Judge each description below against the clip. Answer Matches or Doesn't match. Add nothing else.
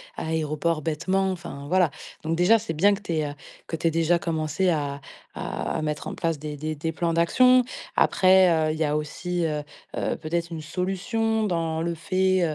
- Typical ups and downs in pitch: Matches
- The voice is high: Doesn't match